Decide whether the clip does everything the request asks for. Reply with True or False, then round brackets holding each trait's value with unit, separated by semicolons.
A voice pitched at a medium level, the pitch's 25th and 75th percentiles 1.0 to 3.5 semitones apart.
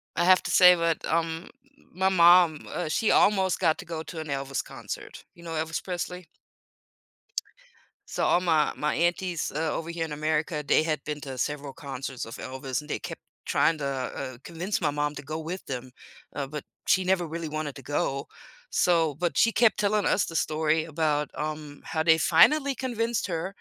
True (160 Hz; 3.0 semitones)